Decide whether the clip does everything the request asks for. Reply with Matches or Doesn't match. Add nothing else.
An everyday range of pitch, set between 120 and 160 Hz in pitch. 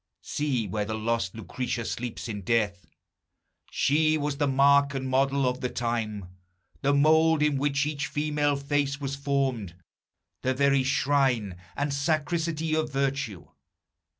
Matches